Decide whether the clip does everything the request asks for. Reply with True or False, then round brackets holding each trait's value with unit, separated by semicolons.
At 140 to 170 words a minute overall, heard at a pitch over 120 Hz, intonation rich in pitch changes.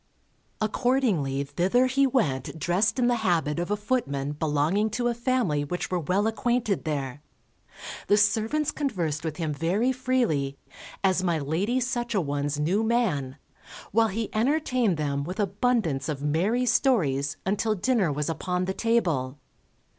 True (150 wpm; 190 Hz; 7.9 semitones)